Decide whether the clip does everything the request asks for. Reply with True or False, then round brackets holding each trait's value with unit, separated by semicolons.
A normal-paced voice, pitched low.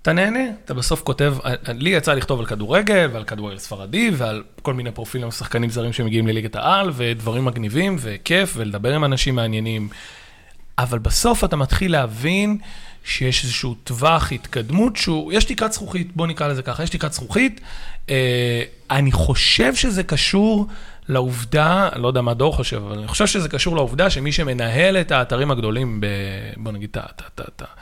False (165 wpm; 130 Hz)